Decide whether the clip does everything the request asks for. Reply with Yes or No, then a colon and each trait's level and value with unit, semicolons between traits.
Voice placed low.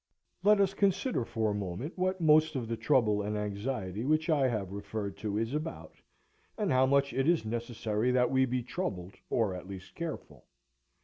Yes: low, 125 Hz